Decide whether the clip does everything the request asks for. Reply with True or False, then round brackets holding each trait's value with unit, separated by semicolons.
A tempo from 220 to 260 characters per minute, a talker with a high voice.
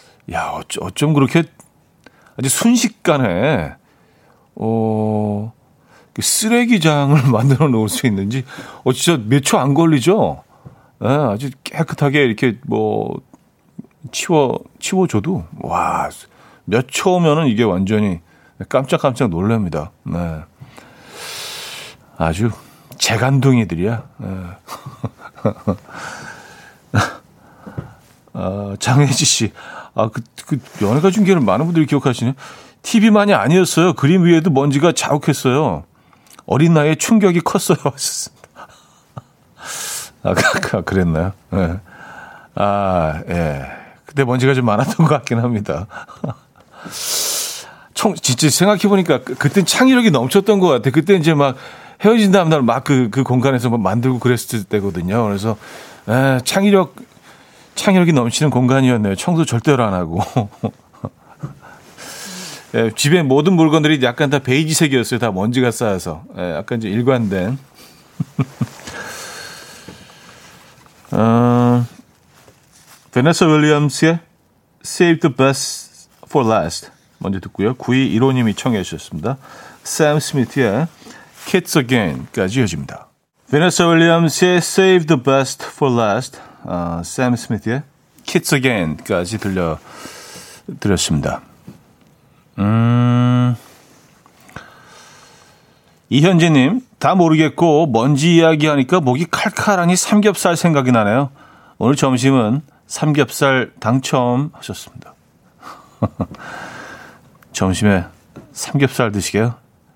False (245 characters per minute; 135 Hz)